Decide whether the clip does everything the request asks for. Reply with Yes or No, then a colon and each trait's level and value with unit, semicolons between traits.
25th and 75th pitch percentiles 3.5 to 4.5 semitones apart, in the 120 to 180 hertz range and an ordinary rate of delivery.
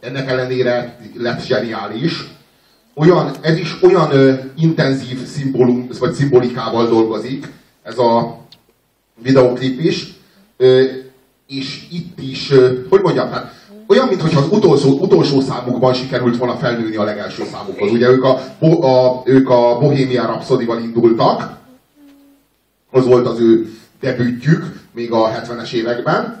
Yes: average, 4.1 semitones; low, 130 Hz; average, 125 wpm